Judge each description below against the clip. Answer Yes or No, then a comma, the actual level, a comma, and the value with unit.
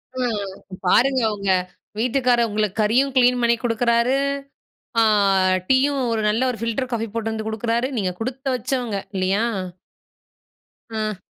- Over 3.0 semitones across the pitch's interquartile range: No, narrow, 2.6 semitones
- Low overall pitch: No, high, 230 Hz